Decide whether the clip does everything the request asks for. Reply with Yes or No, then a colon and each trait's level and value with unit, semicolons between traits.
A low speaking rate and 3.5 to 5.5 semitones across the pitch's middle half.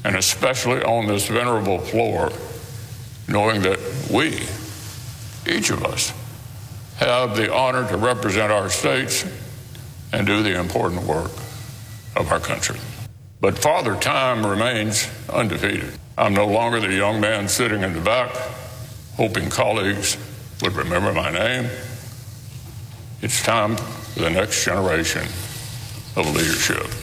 No: slow, 125 wpm; narrow, 2.6 semitones